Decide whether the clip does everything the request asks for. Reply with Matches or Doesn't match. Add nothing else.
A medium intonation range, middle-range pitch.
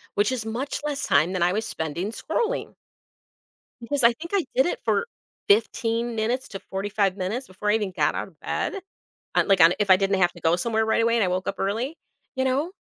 Doesn't match